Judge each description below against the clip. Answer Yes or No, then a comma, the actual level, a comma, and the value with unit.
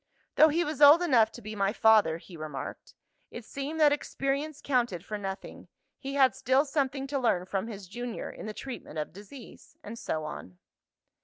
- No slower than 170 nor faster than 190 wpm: Yes, average, 185 wpm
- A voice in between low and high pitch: No, high, 240 Hz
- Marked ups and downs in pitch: Yes, wide, 5.9 semitones